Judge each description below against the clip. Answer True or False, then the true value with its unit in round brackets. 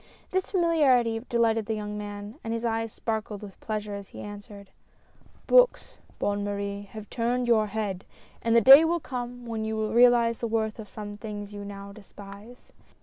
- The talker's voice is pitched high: True (220 Hz)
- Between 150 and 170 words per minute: False (185 wpm)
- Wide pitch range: False (2.5 semitones)